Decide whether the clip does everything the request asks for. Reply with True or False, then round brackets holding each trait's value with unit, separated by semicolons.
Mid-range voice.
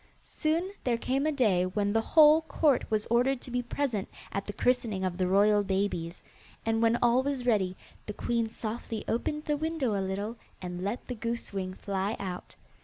False (225 Hz)